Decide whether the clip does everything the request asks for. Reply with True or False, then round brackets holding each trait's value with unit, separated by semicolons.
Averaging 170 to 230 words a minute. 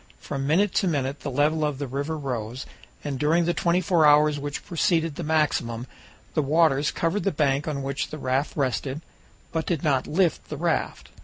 True (190 wpm)